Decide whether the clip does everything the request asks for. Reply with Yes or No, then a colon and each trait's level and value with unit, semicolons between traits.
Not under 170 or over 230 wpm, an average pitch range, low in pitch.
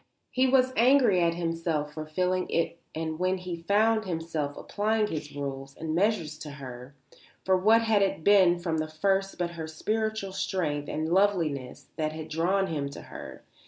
No: average, 175 wpm; average, 4.2 semitones; medium, 170 Hz